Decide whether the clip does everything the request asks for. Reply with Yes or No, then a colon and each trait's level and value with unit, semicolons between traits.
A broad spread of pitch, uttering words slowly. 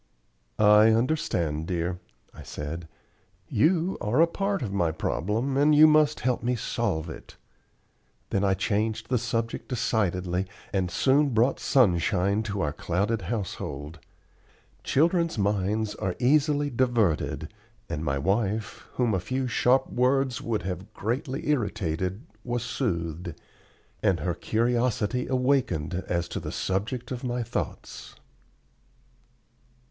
Yes: wide, 5.7 semitones; slow, 125 wpm